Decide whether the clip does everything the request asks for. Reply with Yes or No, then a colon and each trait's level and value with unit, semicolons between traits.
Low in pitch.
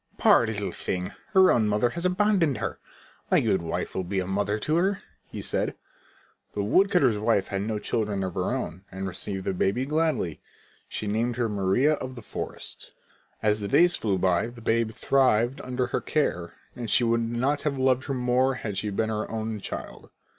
Yes: low, 115 Hz